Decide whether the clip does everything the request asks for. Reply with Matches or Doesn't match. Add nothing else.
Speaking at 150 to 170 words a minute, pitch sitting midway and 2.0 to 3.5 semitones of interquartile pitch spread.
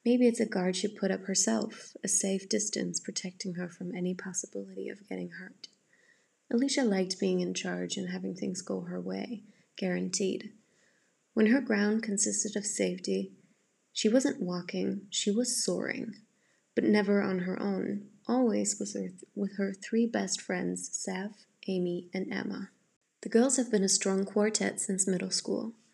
Doesn't match